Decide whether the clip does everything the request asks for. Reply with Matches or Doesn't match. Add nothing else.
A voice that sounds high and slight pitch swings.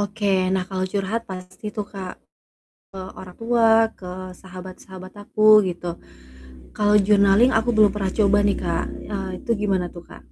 Matches